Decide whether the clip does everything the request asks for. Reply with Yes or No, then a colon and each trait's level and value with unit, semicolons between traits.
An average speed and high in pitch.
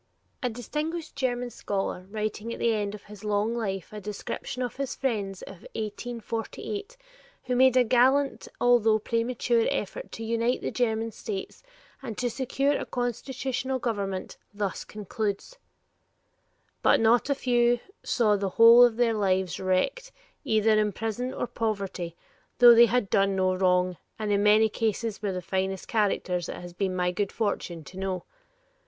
Yes: average, 160 wpm; high, 220 Hz